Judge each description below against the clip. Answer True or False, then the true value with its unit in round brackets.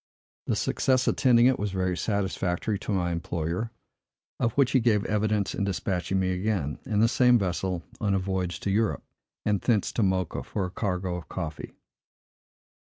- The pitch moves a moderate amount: True (3.2 semitones)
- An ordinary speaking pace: True (170 wpm)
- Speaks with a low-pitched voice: True (100 Hz)